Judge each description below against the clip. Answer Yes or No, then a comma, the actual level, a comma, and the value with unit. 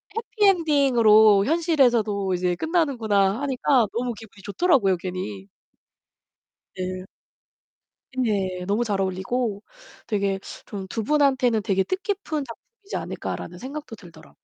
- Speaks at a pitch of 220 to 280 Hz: Yes, high, 225 Hz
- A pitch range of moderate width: No, wide, 6.5 semitones